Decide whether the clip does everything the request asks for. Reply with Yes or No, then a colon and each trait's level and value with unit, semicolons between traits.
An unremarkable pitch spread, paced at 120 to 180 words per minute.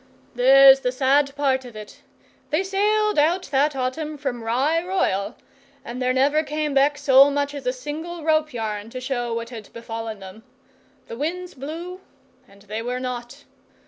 Yes: average, 4.0 semitones; average, 170 wpm